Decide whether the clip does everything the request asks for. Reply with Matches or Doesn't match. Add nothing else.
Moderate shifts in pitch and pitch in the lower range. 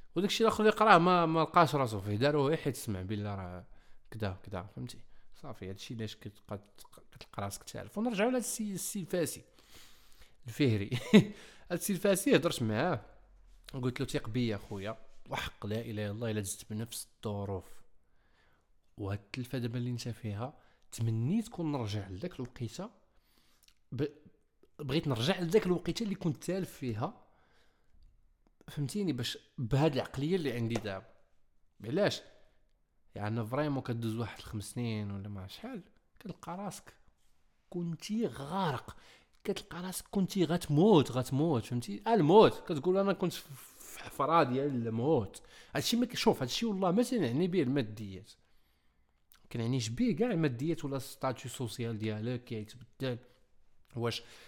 Doesn't match